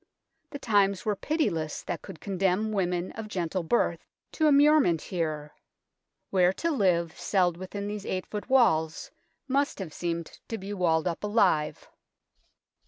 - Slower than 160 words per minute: No, average, 170 wpm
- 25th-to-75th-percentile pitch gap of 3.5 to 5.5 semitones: Yes, average, 4.2 semitones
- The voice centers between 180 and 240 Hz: Yes, high, 190 Hz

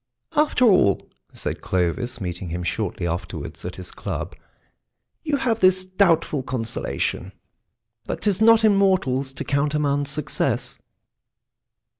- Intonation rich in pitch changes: Yes, wide, 8.5 semitones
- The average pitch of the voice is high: No, medium, 145 Hz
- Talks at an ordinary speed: No, slow, 120 wpm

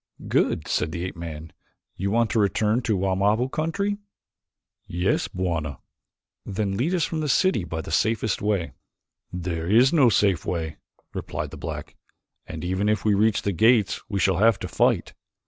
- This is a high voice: No, low, 100 Hz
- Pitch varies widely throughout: No, average, 4.6 semitones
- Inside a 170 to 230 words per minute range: Yes, average, 175 wpm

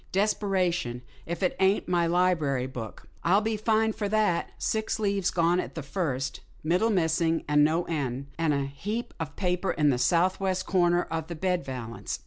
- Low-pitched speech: No, medium, 175 Hz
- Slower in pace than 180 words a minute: No, average, 185 wpm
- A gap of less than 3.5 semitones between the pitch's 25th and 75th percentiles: No, average, 4.5 semitones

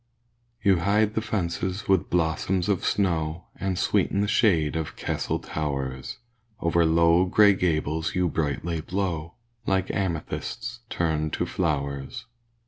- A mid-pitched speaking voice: No, very low, 85 Hz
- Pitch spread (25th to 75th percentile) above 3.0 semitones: Yes, average, 3.6 semitones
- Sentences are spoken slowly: Yes, slow, 130 wpm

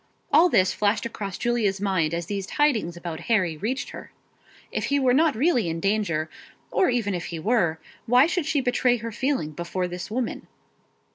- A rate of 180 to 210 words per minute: Yes, average, 185 wpm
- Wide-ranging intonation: Yes, wide, 6.2 semitones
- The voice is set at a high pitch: Yes, high, 210 Hz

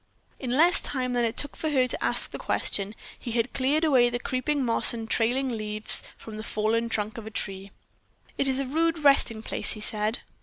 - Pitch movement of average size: Yes, average, 3.7 semitones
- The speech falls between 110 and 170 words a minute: No, fast, 205 wpm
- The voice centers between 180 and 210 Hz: No, high, 240 Hz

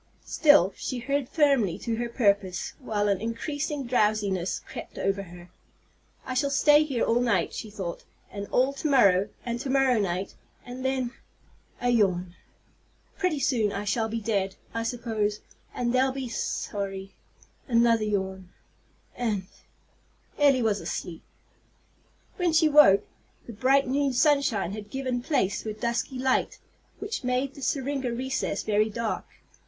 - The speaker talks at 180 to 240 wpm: No, average, 150 wpm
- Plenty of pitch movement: No, average, 4.7 semitones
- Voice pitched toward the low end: No, high, 235 Hz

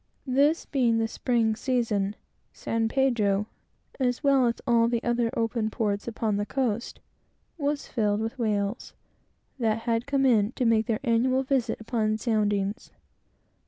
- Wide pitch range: No, average, 2.7 semitones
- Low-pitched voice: No, high, 230 Hz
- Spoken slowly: No, average, 145 wpm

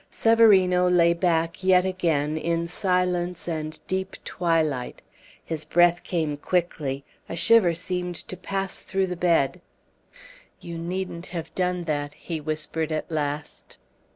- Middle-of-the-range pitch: Yes, medium, 170 Hz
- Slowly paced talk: Yes, slow, 130 wpm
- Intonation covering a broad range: No, narrow, 2.4 semitones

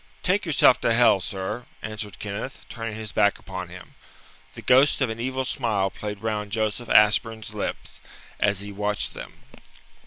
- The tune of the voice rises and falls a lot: No, narrow, 2.5 semitones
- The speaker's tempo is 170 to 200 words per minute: No, average, 160 wpm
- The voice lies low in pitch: Yes, low, 110 Hz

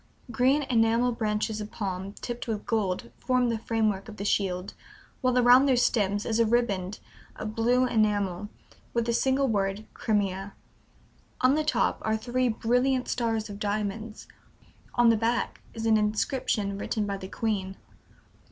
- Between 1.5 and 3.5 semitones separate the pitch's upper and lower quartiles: Yes, average, 2.9 semitones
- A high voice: Yes, high, 220 Hz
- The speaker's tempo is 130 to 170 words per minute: Yes, average, 155 wpm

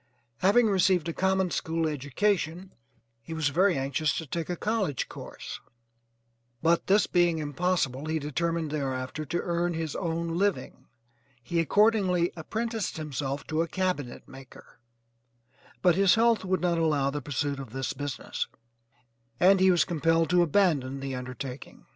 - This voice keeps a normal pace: Yes, average, 150 wpm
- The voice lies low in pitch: No, medium, 165 Hz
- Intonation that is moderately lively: Yes, average, 4.3 semitones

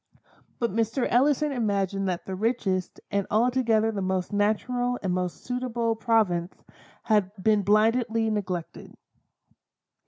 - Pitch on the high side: Yes, high, 215 Hz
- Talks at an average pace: No, slow, 120 wpm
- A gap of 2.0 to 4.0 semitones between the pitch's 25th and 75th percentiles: Yes, average, 3.5 semitones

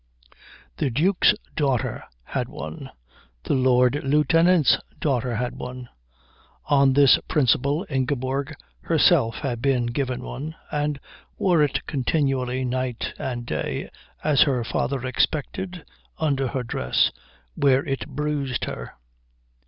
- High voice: No, low, 135 Hz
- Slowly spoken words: Yes, slow, 115 wpm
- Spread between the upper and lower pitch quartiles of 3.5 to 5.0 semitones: No, average, 2.7 semitones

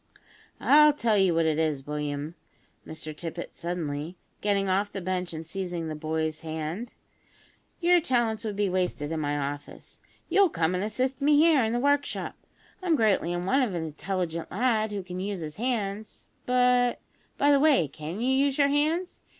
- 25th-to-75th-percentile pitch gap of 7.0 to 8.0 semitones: Yes, wide, 7.6 semitones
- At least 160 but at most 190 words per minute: Yes, average, 185 wpm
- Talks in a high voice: Yes, high, 195 Hz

